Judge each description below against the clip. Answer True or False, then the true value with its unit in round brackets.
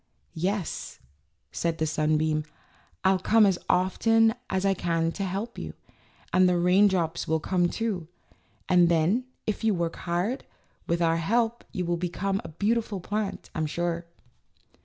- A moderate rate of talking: True (150 wpm)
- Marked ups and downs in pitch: False (3.4 semitones)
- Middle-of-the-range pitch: True (180 Hz)